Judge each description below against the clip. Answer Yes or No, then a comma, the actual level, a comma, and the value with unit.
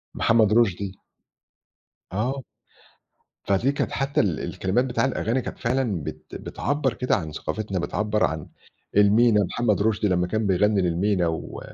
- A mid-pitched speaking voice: No, low, 105 Hz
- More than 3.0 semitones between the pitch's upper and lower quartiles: Yes, average, 4.1 semitones